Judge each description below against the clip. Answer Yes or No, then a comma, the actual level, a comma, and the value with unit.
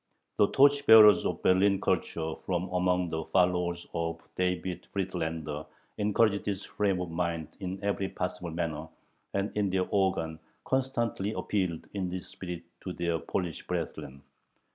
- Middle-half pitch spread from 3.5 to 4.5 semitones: No, average, 2.8 semitones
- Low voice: Yes, very low, 90 Hz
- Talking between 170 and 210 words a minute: No, average, 140 wpm